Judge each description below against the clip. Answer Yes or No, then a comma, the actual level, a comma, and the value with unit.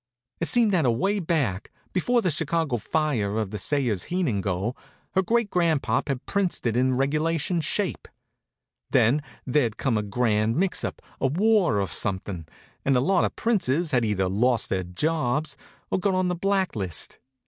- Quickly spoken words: No, average, 170 wpm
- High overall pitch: No, medium, 140 Hz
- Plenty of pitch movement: Yes, wide, 8.3 semitones